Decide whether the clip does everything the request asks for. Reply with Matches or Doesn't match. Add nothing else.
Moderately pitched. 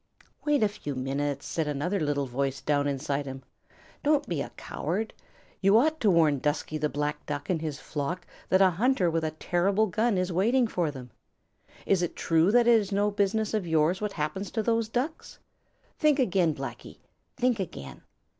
Matches